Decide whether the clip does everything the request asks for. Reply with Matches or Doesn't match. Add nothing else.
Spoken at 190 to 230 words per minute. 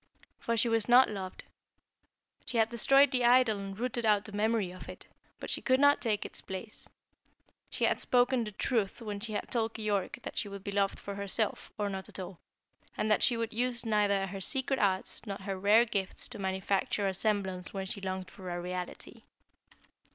Matches